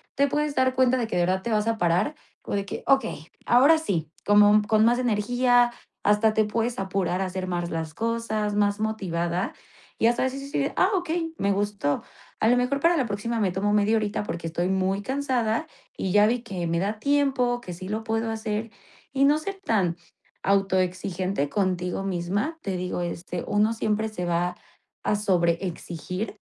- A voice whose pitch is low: No, high, 210 Hz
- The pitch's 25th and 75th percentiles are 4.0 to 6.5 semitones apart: Yes, average, 4.6 semitones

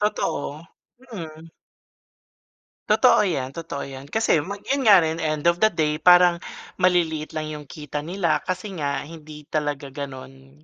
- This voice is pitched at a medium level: Yes, medium, 155 Hz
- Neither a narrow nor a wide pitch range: Yes, average, 3.3 semitones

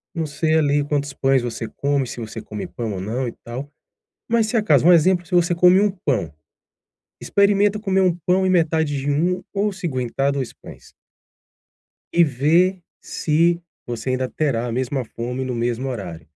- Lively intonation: Yes, wide, 6.1 semitones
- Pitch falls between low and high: Yes, medium, 145 Hz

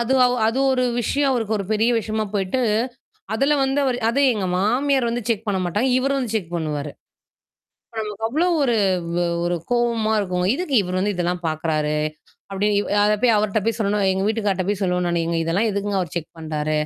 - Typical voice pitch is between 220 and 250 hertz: No, high, 205 Hz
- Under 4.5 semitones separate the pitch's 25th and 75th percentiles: No, average, 4.8 semitones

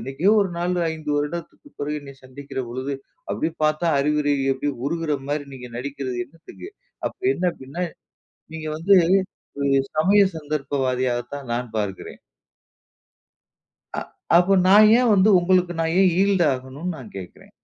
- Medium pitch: Yes, medium, 150 Hz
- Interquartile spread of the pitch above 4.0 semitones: Yes, average, 4.7 semitones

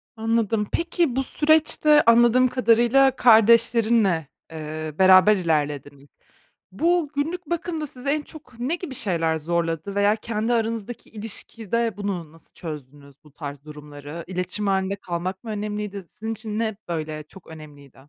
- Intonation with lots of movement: Yes, wide, 6.5 semitones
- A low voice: No, high, 210 Hz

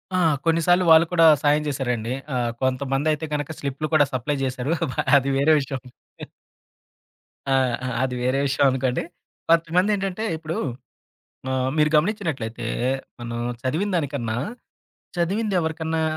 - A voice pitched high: No, medium, 145 Hz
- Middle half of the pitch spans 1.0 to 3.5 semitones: No, average, 4.2 semitones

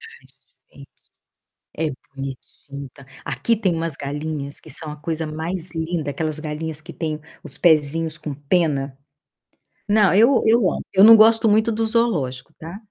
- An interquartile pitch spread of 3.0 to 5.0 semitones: Yes, average, 4.6 semitones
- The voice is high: No, medium, 160 Hz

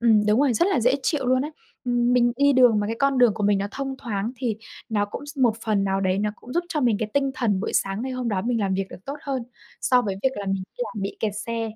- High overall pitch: Yes, high, 230 Hz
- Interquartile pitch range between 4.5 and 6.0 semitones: No, average, 4.0 semitones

